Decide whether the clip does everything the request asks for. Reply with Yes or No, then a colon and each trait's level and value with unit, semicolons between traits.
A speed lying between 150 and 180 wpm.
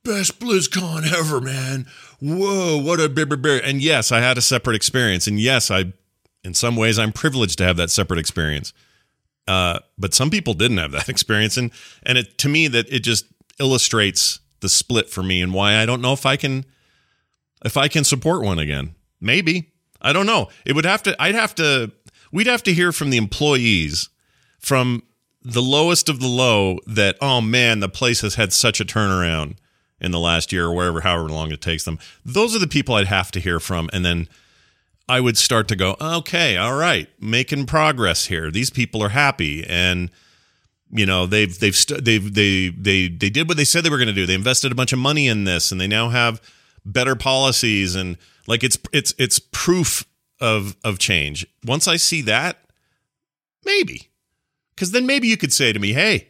No: average, 200 wpm